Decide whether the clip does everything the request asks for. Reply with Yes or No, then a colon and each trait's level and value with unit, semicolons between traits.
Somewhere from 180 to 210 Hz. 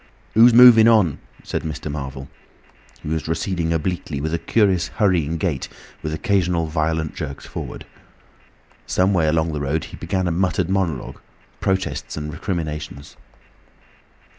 No: very low, 80 Hz